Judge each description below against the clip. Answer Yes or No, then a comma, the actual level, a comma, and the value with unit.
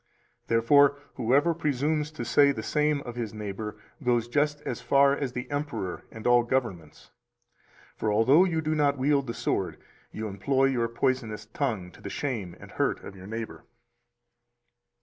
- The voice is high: No, low, 125 Hz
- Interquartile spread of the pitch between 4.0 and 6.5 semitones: Yes, average, 4.5 semitones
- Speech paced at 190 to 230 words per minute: No, average, 165 wpm